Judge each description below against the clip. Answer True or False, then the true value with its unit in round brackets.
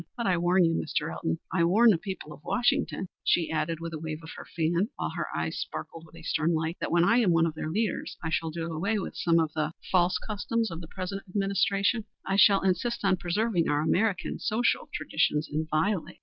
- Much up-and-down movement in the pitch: False (3.6 semitones)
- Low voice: False (175 Hz)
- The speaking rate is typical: False (225 wpm)